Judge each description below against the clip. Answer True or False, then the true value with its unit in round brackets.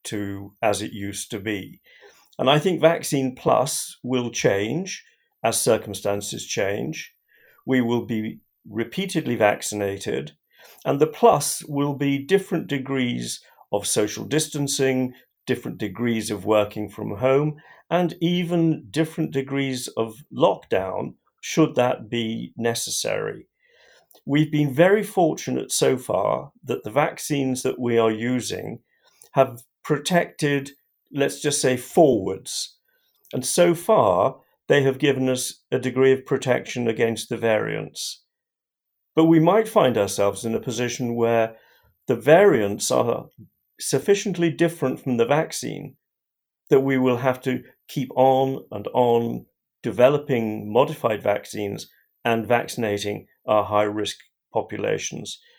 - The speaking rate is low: True (125 wpm)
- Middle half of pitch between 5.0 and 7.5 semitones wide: True (5.3 semitones)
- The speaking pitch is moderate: False (130 Hz)